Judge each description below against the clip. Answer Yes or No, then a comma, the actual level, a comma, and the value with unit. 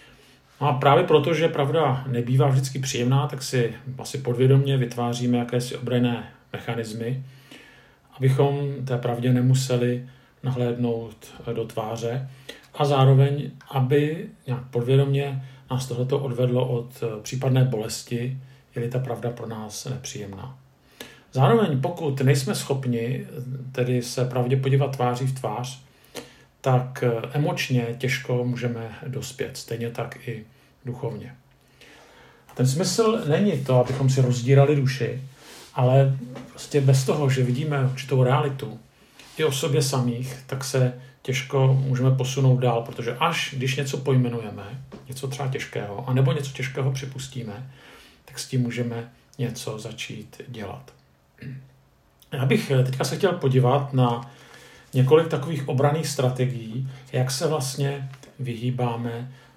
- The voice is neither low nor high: No, low, 130 Hz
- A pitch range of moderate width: No, narrow, 2.0 semitones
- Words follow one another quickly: No, average, 125 wpm